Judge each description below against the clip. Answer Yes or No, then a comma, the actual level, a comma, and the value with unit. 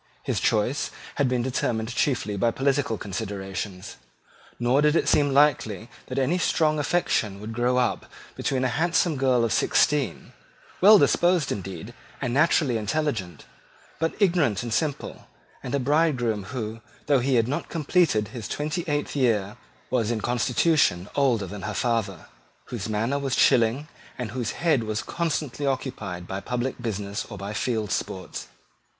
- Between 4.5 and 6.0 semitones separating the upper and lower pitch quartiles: Yes, average, 5.2 semitones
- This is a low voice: Yes, low, 125 Hz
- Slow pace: No, average, 155 wpm